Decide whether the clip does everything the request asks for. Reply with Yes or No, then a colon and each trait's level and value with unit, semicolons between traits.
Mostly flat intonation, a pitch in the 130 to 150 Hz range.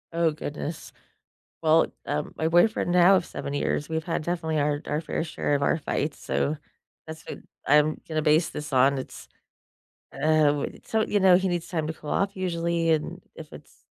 No: narrow, 2.3 semitones; medium, 160 Hz